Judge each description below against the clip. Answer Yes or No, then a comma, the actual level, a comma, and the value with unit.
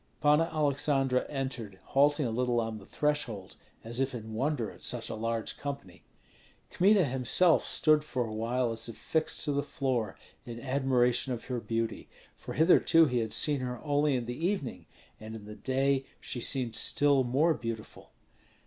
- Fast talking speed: No, average, 175 wpm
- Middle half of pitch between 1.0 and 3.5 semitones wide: No, average, 3.9 semitones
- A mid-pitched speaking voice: No, low, 130 Hz